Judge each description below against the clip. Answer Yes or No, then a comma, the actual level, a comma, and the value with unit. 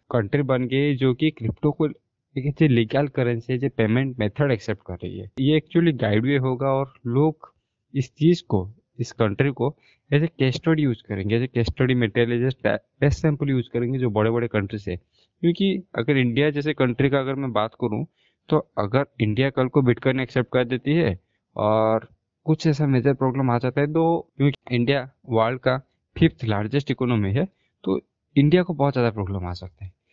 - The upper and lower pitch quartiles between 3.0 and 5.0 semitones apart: Yes, average, 4.0 semitones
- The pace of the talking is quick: Yes, fast, 195 wpm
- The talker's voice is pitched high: No, low, 130 Hz